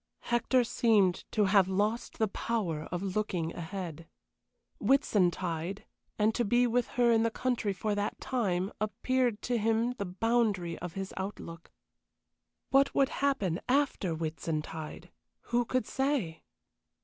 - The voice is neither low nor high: No, high, 210 Hz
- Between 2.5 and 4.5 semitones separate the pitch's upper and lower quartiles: No, average, 5.0 semitones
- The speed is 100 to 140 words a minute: Yes, slow, 135 wpm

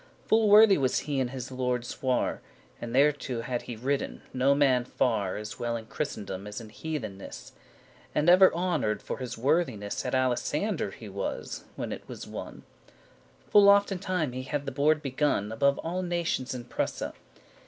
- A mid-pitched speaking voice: No, low, 130 Hz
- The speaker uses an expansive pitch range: No, average, 4.8 semitones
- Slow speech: No, average, 175 wpm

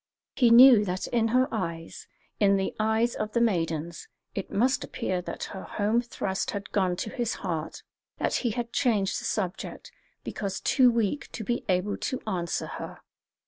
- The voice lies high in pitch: Yes, high, 210 Hz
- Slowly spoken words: No, average, 175 wpm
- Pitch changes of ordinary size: Yes, average, 4.0 semitones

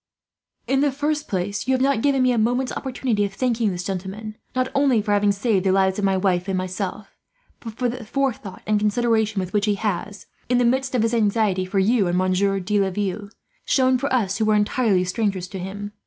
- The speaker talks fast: Yes, fast, 220 wpm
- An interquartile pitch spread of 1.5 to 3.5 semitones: No, average, 4.2 semitones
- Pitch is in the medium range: No, high, 210 Hz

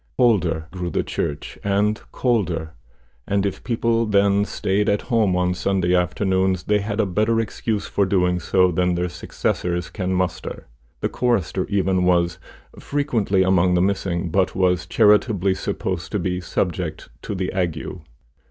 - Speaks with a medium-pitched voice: No, very low, 95 Hz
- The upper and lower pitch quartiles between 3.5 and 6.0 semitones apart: No, narrow, 2.5 semitones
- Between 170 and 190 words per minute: No, average, 150 wpm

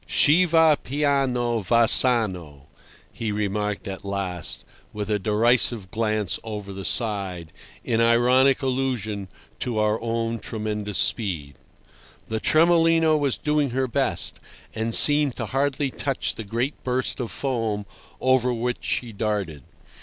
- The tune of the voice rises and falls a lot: No, average, 4.1 semitones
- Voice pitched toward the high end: No, low, 115 Hz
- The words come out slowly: Yes, slow, 130 wpm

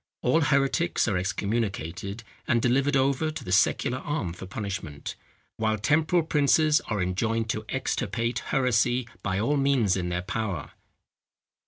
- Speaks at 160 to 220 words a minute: No, average, 140 wpm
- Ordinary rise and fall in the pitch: No, wide, 5.9 semitones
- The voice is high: No, low, 115 Hz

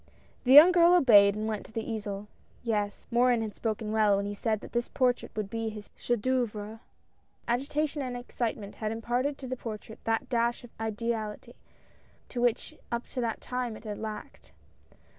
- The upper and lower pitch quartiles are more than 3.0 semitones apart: No, narrow, 2.4 semitones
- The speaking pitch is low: No, high, 225 Hz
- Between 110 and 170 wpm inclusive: No, average, 180 wpm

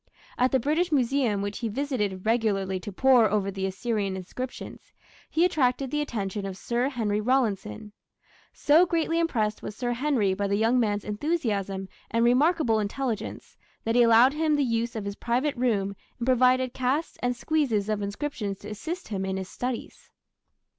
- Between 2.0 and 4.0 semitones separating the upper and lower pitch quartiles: No, average, 4.6 semitones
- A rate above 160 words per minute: Yes, average, 170 wpm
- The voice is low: No, high, 235 Hz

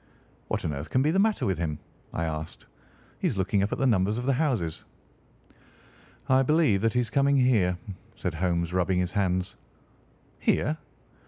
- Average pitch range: No, wide, 6.7 semitones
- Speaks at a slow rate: No, average, 180 wpm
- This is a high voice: No, low, 100 Hz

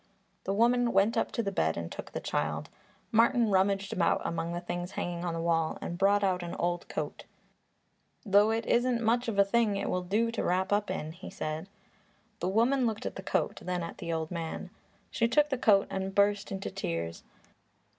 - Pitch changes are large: No, average, 4.4 semitones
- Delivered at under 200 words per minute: No, fast, 205 wpm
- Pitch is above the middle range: Yes, high, 195 Hz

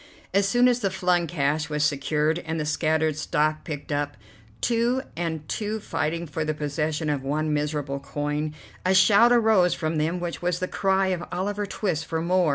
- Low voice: No, medium, 160 Hz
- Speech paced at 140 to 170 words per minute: No, average, 185 wpm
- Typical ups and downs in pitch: Yes, average, 3.9 semitones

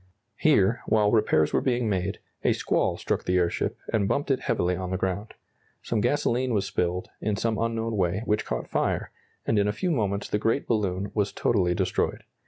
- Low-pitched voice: Yes, low, 105 Hz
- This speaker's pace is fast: No, average, 190 wpm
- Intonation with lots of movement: No, average, 3.4 semitones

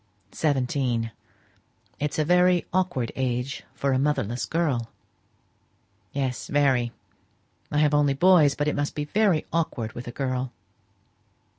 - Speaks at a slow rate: Yes, slow, 130 wpm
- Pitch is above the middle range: No, medium, 140 Hz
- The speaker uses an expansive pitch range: No, average, 3.4 semitones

